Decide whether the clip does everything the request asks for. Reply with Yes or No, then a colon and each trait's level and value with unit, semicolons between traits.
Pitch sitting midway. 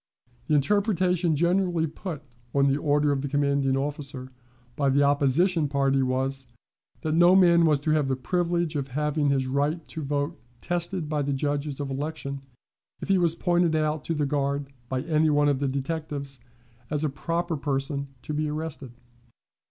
Yes: medium, 150 Hz